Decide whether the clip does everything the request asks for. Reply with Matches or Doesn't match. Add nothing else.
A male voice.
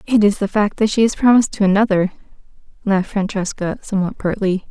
Doesn't match